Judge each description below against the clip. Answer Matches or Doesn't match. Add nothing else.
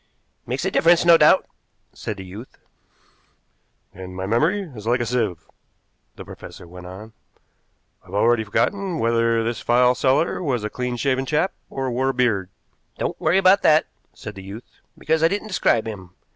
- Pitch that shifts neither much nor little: Doesn't match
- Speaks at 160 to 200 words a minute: Matches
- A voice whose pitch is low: Matches